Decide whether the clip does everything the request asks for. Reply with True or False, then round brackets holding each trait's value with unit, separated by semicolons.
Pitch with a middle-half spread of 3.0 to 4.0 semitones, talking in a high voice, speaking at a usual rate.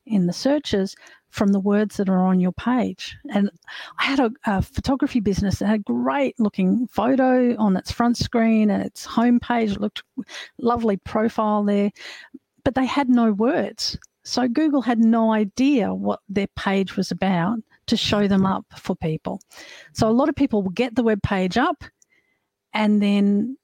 True (3.6 semitones; 220 Hz; 180 wpm)